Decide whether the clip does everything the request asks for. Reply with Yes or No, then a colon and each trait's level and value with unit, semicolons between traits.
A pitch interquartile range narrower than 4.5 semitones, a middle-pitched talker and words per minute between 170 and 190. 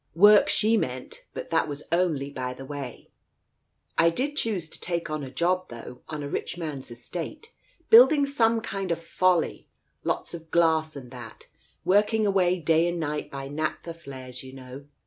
No: average, 5.0 semitones; medium, 165 Hz; average, 180 wpm